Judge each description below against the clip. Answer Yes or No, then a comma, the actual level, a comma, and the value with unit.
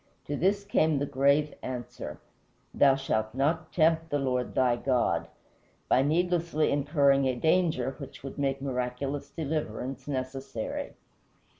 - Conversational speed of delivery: No, slow, 130 wpm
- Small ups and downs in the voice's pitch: No, average, 3.2 semitones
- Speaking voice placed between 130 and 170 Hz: Yes, medium, 140 Hz